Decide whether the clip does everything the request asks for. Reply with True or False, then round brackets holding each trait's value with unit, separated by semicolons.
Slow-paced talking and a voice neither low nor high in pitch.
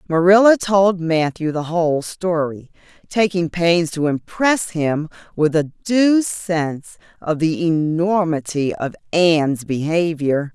True (120 wpm; 165 Hz)